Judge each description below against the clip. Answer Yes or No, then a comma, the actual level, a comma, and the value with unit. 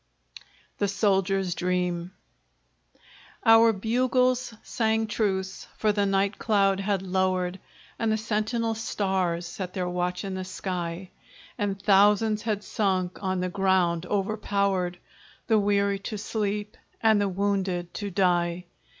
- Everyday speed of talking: No, slow, 125 wpm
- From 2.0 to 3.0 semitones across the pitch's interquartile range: Yes, narrow, 2.4 semitones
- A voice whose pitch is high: Yes, high, 195 Hz